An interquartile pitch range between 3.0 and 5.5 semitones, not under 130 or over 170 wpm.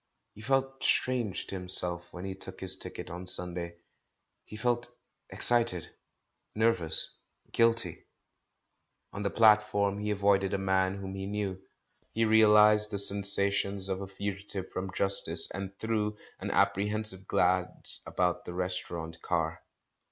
No: narrow, 2.4 semitones; slow, 135 wpm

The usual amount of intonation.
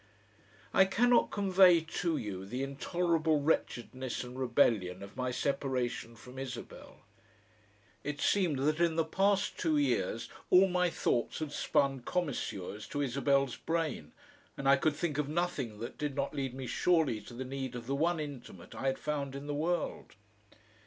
Yes: average, 4.6 semitones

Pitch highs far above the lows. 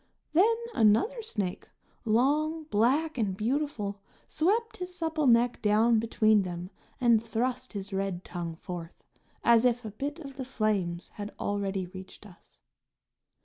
Yes: wide, 6.1 semitones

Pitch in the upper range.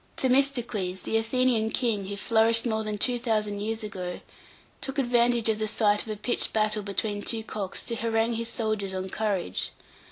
Yes: high, 220 Hz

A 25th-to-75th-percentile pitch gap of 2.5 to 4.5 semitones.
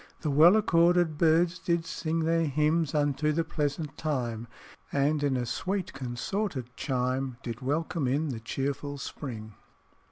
Yes: average, 3.9 semitones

